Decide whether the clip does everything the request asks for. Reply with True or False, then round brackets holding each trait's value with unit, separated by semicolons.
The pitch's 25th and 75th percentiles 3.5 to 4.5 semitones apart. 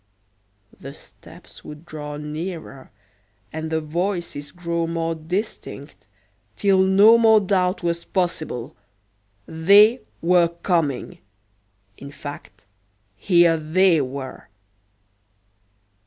True (3.8 semitones)